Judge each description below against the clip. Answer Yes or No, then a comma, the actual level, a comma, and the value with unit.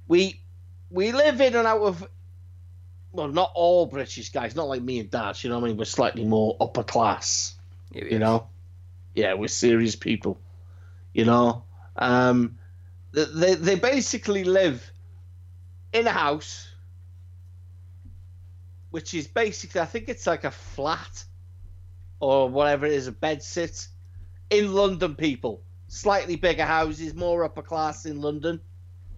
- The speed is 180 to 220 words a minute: No, average, 145 wpm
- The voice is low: Yes, low, 110 Hz